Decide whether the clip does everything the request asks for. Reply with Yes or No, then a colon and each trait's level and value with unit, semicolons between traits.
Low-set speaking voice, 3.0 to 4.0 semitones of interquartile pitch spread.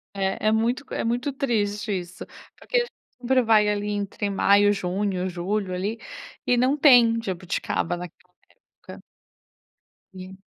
No: high, 205 Hz; average, 3.7 semitones